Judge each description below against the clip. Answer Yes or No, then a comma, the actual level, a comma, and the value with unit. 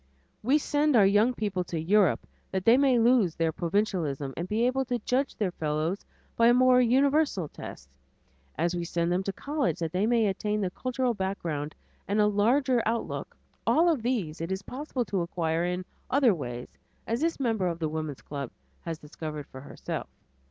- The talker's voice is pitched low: No, high, 200 Hz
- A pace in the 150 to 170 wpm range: No, average, 185 wpm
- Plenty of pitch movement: Yes, wide, 6.8 semitones